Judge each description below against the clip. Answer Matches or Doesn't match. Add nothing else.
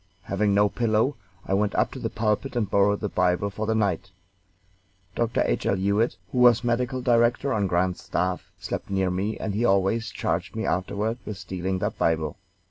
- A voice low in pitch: Matches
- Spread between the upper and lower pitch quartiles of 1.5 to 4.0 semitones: Matches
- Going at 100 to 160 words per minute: Doesn't match